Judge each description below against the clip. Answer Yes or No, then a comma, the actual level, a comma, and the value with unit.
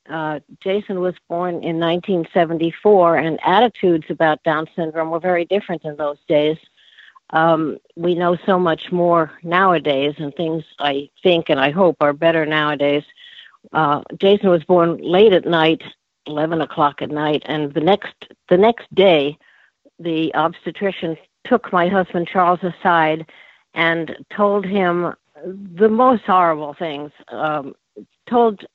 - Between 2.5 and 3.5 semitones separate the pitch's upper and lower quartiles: Yes, average, 2.9 semitones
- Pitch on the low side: No, medium, 170 Hz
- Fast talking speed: No, average, 140 wpm